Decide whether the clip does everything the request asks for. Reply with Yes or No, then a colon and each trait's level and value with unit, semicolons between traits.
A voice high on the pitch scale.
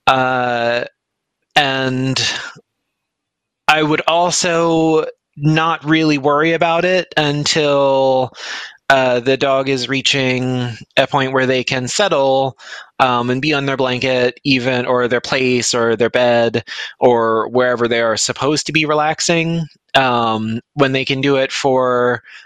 No: low, 135 Hz